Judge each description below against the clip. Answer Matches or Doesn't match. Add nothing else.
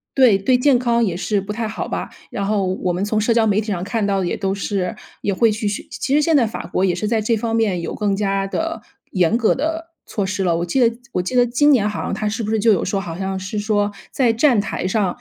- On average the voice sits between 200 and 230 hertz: Matches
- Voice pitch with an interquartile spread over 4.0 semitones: Doesn't match